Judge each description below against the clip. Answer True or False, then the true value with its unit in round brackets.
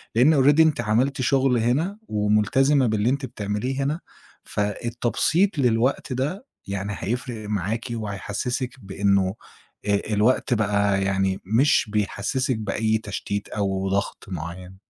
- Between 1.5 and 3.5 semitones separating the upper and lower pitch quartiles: False (4.5 semitones)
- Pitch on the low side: True (110 Hz)